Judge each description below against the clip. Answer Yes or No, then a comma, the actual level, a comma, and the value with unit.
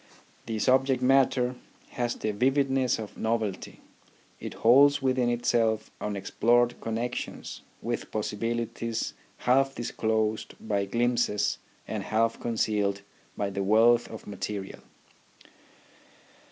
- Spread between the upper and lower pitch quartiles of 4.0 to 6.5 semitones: No, narrow, 2.5 semitones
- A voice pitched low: Yes, low, 115 Hz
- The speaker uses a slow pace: Yes, slow, 100 wpm